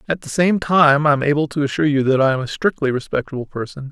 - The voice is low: No, medium, 145 Hz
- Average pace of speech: No, fast, 260 wpm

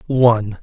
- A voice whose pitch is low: Yes, low, 115 Hz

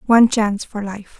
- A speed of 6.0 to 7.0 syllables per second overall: No, 5.8 syllables/s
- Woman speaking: Yes, female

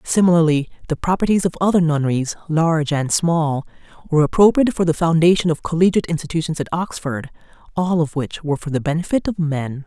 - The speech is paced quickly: No, average, 170 wpm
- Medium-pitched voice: Yes, medium, 165 Hz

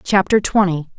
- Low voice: No, medium, 185 Hz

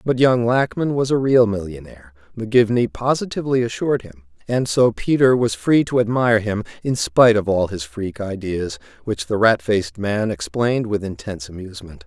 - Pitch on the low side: Yes, low, 110 Hz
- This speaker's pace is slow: No, average, 175 wpm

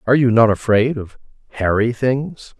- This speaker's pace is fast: No, average, 160 wpm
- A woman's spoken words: No, male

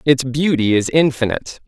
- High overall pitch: No, low, 130 Hz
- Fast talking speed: No, average, 145 wpm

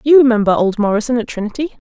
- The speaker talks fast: No, average, 190 wpm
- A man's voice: No, female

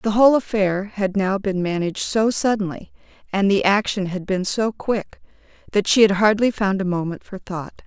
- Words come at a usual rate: Yes, average, 190 wpm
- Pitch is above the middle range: Yes, high, 200 Hz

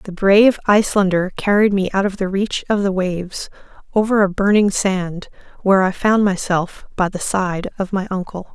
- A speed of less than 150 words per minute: No, average, 185 wpm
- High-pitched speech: Yes, high, 195 Hz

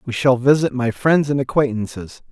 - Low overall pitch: Yes, low, 125 Hz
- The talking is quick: No, average, 180 wpm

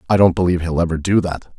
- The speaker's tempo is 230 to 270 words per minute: Yes, fast, 265 wpm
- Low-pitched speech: Yes, very low, 85 Hz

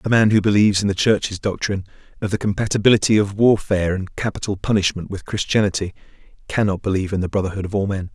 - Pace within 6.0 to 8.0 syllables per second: Yes, 6.8 syllables/s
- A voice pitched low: Yes, low, 100 Hz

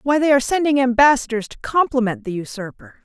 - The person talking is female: Yes, female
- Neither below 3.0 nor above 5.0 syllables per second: No, 6.2 syllables/s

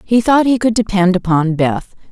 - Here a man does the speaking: No, female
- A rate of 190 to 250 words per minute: Yes, average, 200 wpm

